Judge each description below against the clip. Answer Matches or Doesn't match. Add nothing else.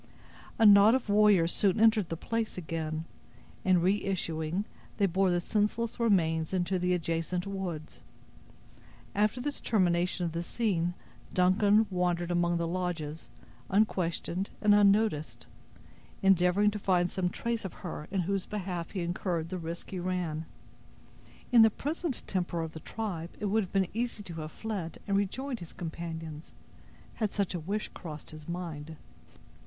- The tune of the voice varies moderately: Matches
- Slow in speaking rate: Doesn't match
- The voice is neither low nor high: Matches